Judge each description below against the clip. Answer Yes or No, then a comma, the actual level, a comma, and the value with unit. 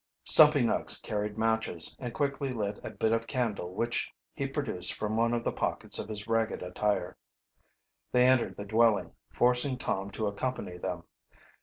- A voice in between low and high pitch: No, low, 115 Hz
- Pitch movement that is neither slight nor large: Yes, average, 3.3 semitones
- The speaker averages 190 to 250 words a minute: No, average, 165 wpm